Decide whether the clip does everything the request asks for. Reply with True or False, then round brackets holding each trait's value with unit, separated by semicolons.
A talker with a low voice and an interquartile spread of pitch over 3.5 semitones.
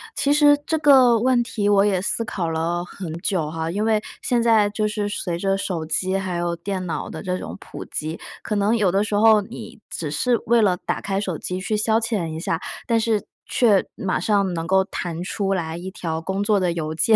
False (195 Hz; 3.9 semitones)